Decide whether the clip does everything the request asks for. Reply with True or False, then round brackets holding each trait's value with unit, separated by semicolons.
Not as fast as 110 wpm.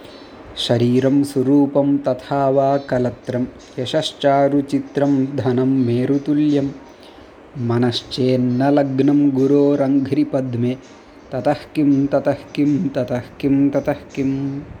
True (75 wpm)